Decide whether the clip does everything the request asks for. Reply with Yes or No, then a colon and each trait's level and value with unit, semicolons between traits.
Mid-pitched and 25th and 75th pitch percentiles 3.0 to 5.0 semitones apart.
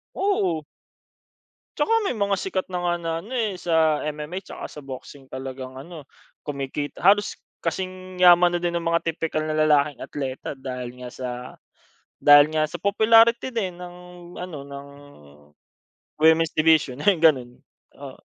Yes: medium, 160 Hz; average, 4.3 semitones